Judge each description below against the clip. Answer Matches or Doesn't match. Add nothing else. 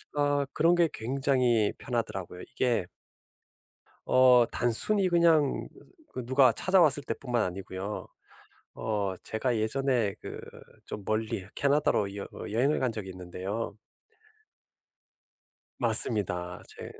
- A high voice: Doesn't match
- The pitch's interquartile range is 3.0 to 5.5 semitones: Matches